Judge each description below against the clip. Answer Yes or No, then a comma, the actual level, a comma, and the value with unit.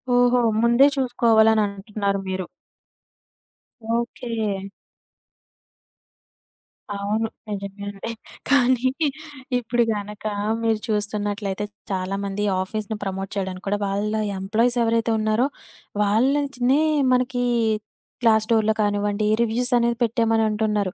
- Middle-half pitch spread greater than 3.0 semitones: No, average, 2.7 semitones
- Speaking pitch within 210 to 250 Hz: Yes, high, 215 Hz